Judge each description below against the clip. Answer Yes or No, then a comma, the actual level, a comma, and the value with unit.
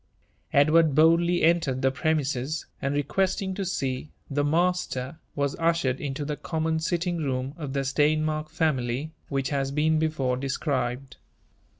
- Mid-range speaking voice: Yes, medium, 150 Hz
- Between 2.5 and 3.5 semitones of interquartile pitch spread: Yes, average, 3.1 semitones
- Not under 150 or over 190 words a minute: No, average, 140 wpm